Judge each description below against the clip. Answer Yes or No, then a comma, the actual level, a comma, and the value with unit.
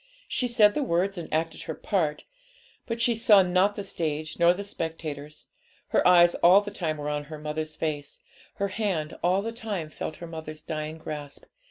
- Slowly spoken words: No, average, 190 wpm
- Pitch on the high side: No, medium, 170 Hz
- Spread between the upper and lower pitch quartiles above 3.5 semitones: Yes, average, 4.5 semitones